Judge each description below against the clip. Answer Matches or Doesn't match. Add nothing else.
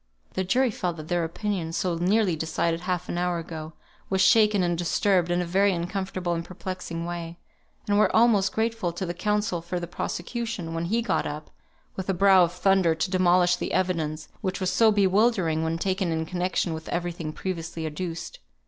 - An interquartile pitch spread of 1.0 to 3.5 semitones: Matches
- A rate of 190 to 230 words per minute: Matches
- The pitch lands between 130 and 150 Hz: Doesn't match